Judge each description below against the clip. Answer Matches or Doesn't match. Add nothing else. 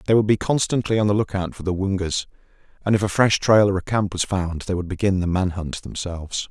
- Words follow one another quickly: Matches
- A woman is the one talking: Doesn't match